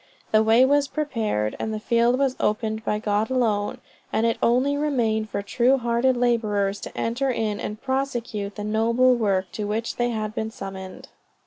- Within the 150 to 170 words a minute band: No, average, 180 wpm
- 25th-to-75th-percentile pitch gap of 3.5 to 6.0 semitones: No, average, 2.9 semitones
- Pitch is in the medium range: No, high, 225 Hz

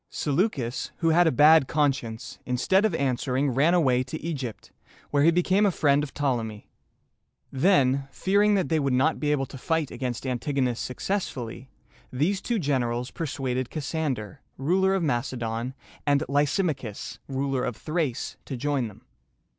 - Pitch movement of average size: Yes, average, 4.3 semitones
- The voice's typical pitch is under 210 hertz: Yes, medium, 140 Hz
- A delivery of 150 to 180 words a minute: Yes, average, 155 wpm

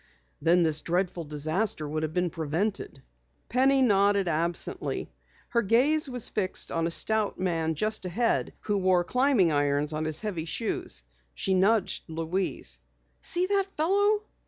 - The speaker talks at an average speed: Yes, average, 145 wpm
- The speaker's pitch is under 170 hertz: No, medium, 185 Hz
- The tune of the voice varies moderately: No, wide, 5.9 semitones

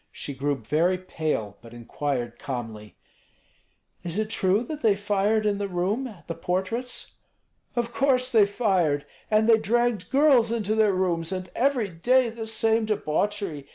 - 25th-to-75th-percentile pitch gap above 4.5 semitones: Yes, wide, 5.5 semitones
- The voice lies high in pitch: Yes, high, 200 Hz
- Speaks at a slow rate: No, average, 155 wpm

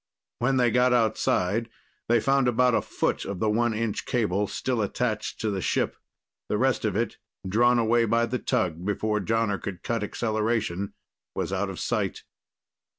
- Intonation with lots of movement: No, narrow, 2.5 semitones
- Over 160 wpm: Yes, average, 170 wpm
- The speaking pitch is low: Yes, low, 115 Hz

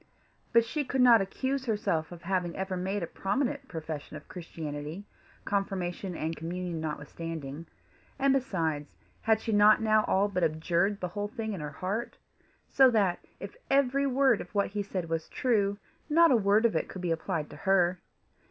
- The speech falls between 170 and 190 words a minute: Yes, average, 180 wpm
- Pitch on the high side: Yes, high, 195 Hz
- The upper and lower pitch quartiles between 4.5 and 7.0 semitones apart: Yes, average, 5.0 semitones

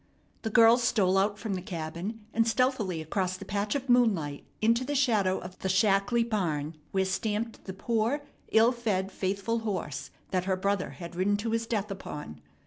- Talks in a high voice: Yes, high, 205 Hz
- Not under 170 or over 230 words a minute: Yes, average, 180 wpm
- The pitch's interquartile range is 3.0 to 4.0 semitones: Yes, average, 3.5 semitones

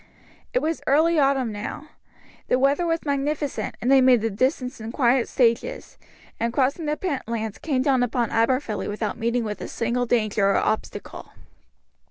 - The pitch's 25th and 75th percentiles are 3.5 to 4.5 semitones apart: Yes, average, 3.8 semitones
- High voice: Yes, very high, 255 Hz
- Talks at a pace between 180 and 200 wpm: No, average, 165 wpm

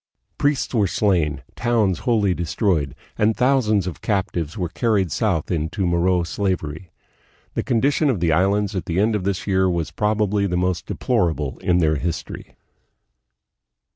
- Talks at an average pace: Yes, average, 150 wpm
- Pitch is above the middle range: No, very low, 95 Hz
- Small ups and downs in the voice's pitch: No, average, 3.7 semitones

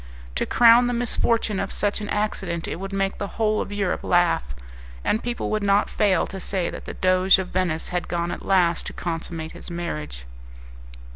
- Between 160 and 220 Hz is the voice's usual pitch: Yes, high, 190 Hz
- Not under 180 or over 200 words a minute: Yes, average, 195 wpm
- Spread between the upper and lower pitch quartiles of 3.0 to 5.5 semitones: Yes, average, 3.3 semitones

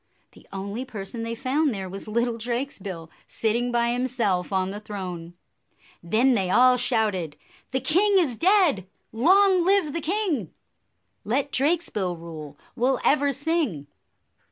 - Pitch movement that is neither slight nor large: No, wide, 6.7 semitones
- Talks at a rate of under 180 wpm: Yes, average, 145 wpm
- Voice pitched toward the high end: Yes, high, 235 Hz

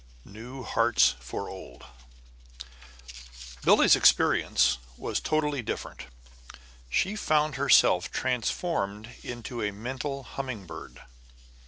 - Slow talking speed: Yes, slow, 100 wpm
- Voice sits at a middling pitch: No, low, 125 Hz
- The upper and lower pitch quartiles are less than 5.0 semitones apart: No, average, 5.3 semitones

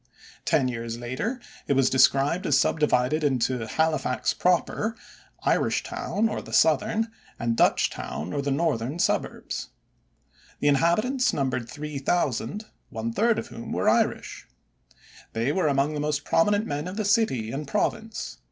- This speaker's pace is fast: No, average, 140 wpm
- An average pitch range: No, wide, 6.1 semitones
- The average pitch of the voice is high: No, medium, 145 Hz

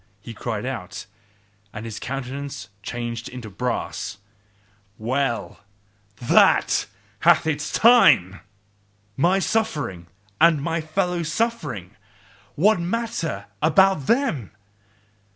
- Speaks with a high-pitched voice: No, medium, 140 Hz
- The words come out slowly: Yes, slow, 100 wpm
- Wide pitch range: Yes, wide, 7.3 semitones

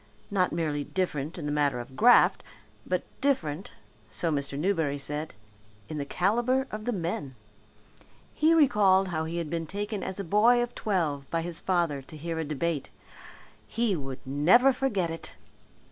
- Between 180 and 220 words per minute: No, average, 165 wpm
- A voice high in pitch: No, medium, 170 Hz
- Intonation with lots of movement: Yes, wide, 5.7 semitones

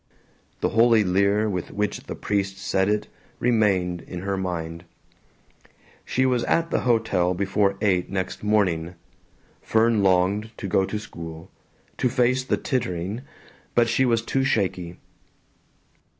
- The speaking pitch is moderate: No, low, 100 Hz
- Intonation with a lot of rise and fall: No, average, 3.8 semitones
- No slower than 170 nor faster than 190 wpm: No, slow, 135 wpm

